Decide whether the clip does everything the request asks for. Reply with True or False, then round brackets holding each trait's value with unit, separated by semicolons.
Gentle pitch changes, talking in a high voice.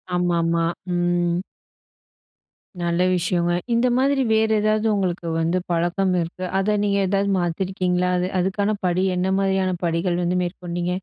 False (2.1 semitones; 180 Hz)